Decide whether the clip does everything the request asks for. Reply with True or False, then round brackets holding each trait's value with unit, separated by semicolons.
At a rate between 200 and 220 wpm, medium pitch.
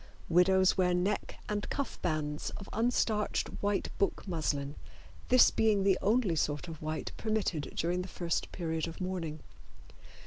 False (145 wpm; 180 Hz)